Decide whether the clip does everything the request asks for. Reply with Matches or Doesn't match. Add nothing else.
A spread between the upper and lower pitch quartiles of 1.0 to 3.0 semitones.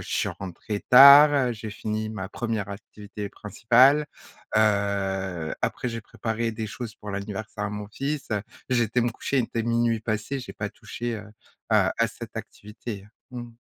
Matches